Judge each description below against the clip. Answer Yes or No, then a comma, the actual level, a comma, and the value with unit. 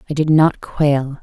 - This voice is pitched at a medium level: Yes, medium, 145 Hz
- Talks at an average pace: Yes, average, 195 wpm